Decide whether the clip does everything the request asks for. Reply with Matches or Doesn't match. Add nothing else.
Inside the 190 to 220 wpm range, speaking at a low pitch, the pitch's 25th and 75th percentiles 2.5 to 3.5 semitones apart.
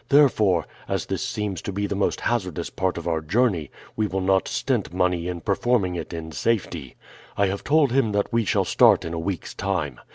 Doesn't match